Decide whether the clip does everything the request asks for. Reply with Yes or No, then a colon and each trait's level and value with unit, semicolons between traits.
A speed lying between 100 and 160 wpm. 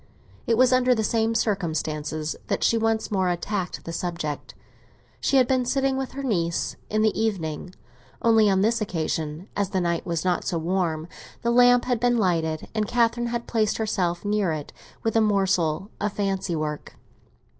No: average, 175 wpm